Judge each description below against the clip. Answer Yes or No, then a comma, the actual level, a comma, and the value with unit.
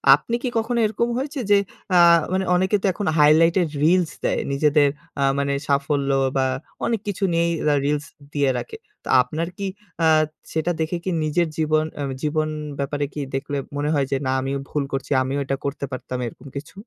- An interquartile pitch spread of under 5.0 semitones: Yes, average, 4.1 semitones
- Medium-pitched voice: Yes, medium, 155 Hz